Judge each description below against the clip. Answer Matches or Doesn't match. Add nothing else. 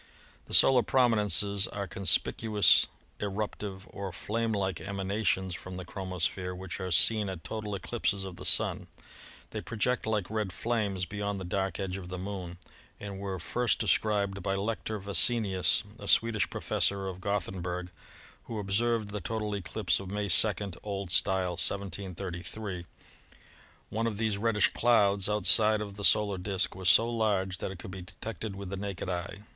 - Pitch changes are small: Matches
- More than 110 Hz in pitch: Doesn't match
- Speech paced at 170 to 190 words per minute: Doesn't match